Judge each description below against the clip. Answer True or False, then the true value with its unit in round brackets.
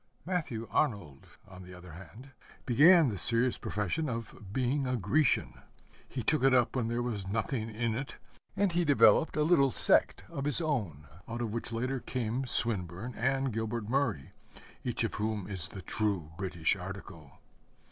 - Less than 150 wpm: False (165 wpm)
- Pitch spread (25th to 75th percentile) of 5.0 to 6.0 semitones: True (5.4 semitones)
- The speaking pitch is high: False (115 Hz)